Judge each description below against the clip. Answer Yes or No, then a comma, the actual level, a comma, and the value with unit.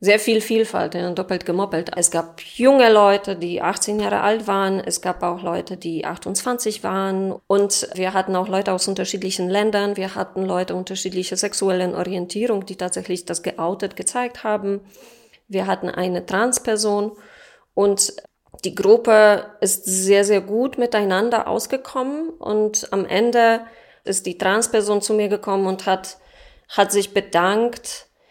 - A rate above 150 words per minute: No, average, 145 wpm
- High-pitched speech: Yes, high, 200 Hz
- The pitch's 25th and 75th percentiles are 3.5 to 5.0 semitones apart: No, average, 2.7 semitones